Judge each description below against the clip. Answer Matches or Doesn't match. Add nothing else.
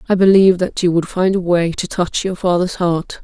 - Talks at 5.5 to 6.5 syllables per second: Doesn't match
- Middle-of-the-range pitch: Matches